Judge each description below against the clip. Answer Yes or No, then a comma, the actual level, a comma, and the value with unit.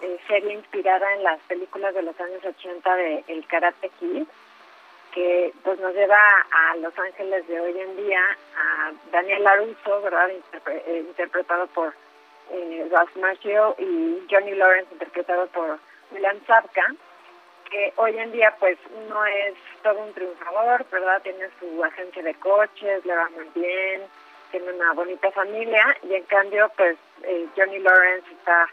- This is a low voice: No, medium, 185 Hz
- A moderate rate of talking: Yes, average, 150 wpm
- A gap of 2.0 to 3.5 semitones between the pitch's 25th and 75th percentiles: Yes, narrow, 2.4 semitones